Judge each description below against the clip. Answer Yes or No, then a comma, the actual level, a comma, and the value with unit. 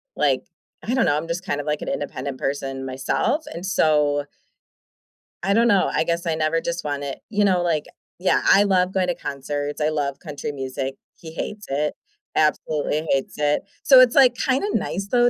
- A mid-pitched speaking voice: Yes, medium, 155 Hz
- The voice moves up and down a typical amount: Yes, average, 5.0 semitones